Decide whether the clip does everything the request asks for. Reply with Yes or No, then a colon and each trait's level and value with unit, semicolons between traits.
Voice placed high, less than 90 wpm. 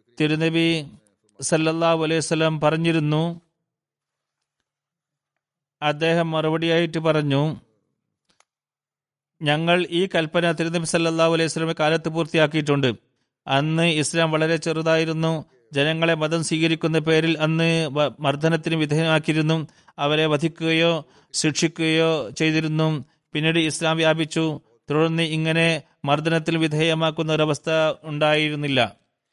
No: medium, 160 Hz; average, 80 wpm